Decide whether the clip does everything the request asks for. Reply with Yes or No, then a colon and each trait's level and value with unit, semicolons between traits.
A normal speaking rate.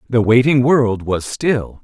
Yes: average, 165 wpm